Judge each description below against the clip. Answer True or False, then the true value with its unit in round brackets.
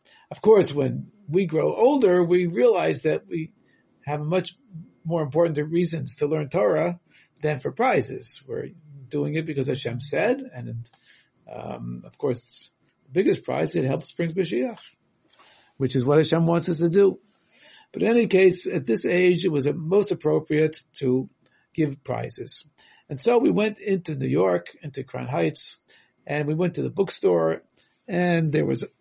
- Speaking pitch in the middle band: True (160 Hz)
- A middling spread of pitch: True (3.7 semitones)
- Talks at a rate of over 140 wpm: True (165 wpm)